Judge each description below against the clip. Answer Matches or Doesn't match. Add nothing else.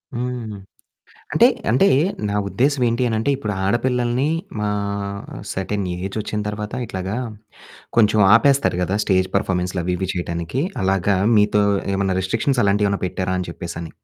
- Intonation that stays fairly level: Doesn't match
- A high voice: Doesn't match